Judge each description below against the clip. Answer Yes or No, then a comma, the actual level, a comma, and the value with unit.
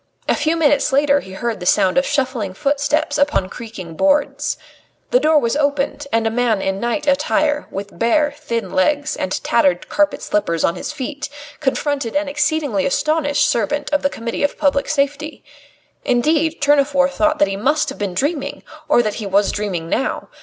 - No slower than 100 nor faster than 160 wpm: No, average, 180 wpm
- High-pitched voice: Yes, very high, 275 Hz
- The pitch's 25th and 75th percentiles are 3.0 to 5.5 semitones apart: Yes, average, 5.2 semitones